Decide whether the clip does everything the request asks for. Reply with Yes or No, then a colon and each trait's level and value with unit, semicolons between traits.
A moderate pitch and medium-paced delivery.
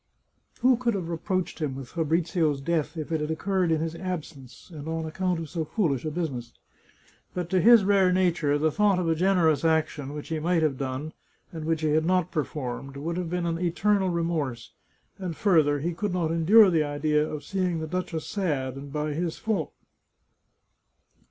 Yes: medium, 165 Hz; average, 195 wpm